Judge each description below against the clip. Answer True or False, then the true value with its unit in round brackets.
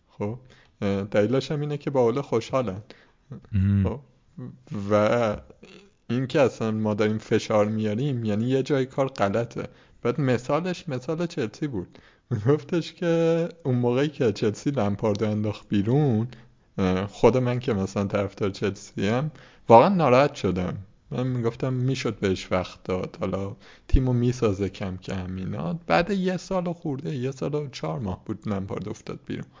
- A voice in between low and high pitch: False (120 Hz)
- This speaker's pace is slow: False (145 wpm)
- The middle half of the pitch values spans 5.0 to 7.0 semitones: True (5.5 semitones)